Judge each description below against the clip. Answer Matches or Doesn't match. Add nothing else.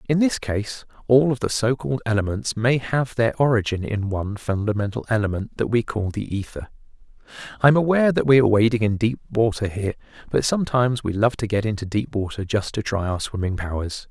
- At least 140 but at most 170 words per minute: Doesn't match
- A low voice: Matches